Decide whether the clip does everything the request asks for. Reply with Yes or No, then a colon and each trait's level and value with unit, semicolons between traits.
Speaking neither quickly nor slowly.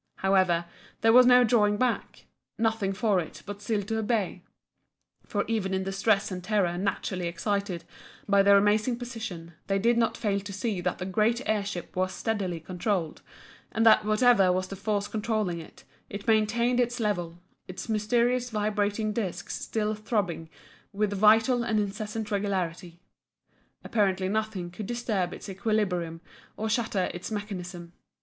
Yes: average, 155 wpm